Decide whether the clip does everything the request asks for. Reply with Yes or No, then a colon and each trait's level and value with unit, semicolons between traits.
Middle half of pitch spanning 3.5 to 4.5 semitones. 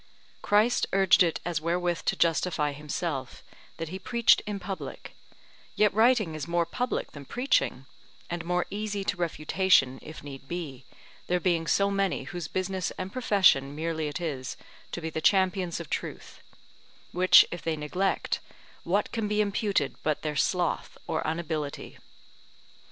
Yes: average, 3.9 semitones